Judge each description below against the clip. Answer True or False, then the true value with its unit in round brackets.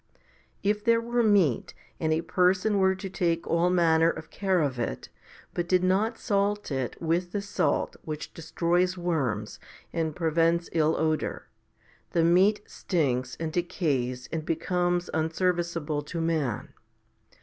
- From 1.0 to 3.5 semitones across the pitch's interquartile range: True (2.8 semitones)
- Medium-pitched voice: True (170 Hz)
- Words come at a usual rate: True (150 wpm)